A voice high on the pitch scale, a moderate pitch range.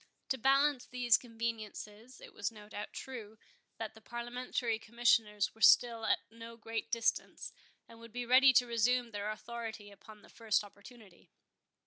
No: high, 230 Hz; narrow, 2.1 semitones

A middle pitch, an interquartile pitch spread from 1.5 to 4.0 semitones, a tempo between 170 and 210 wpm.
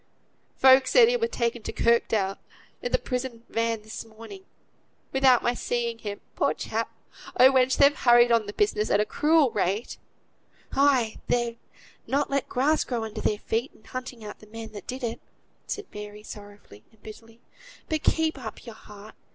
No: high, 235 Hz; average, 3.4 semitones; average, 180 wpm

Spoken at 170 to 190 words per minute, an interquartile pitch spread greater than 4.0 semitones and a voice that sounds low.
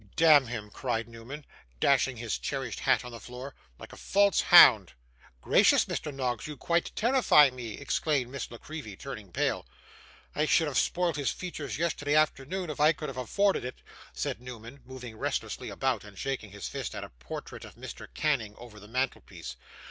Yes: average, 180 wpm; average, 4.5 semitones; low, 130 Hz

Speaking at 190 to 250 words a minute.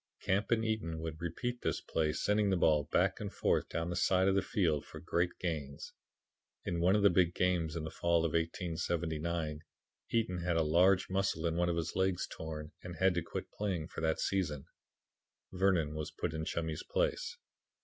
Yes: average, 195 wpm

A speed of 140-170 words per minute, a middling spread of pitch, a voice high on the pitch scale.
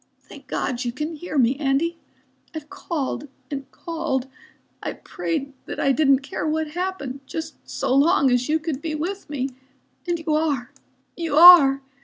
Yes: average, 165 wpm; average, 3.3 semitones; very high, 300 Hz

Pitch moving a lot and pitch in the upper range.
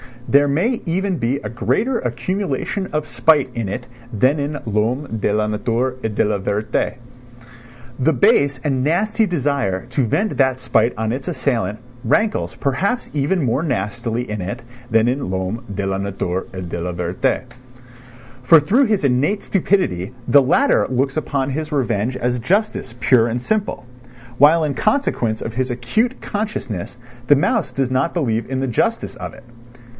No: wide, 5.7 semitones; low, 130 Hz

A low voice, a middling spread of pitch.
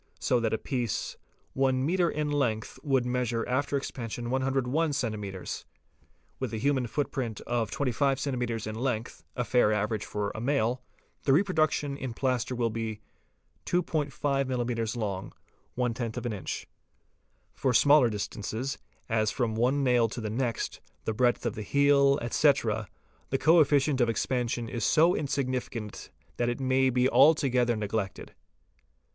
Yes: low, 125 Hz; average, 3.3 semitones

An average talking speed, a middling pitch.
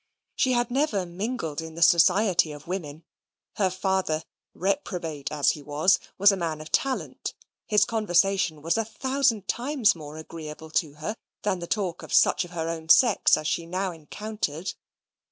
Yes: average, 170 wpm; medium, 180 Hz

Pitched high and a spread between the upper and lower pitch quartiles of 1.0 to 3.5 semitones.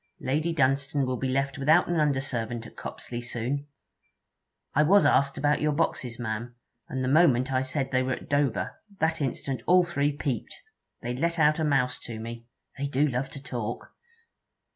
No: low, 135 Hz; average, 2.9 semitones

